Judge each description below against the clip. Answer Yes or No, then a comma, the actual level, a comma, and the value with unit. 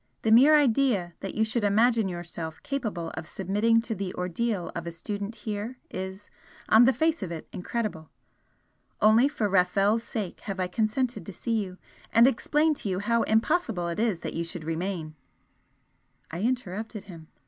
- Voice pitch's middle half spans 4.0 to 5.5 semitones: Yes, average, 4.4 semitones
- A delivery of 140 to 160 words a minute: No, average, 175 wpm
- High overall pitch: Yes, high, 210 Hz